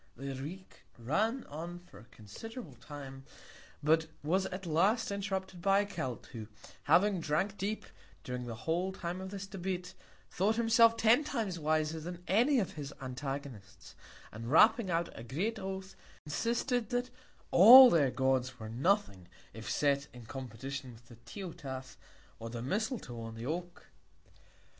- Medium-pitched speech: Yes, medium, 170 Hz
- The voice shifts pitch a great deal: Yes, wide, 7.2 semitones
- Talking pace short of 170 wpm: Yes, average, 150 wpm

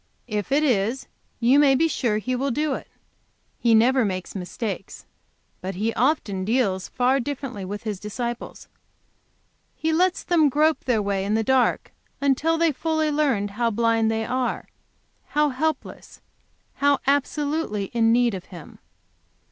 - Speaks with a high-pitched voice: Yes, high, 245 Hz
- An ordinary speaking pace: Yes, average, 150 wpm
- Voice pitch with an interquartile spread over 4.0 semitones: Yes, average, 5.2 semitones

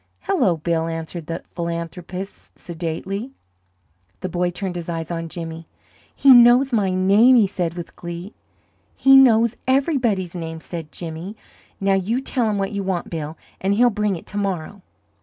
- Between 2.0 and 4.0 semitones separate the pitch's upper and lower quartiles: No, average, 4.5 semitones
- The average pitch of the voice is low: No, medium, 185 Hz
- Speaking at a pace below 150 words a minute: No, average, 160 wpm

